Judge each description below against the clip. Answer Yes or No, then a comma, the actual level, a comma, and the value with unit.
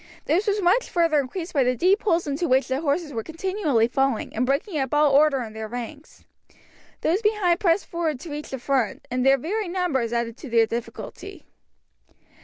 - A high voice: Yes, very high, 290 Hz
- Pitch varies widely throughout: Yes, wide, 5.7 semitones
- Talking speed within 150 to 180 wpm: No, average, 195 wpm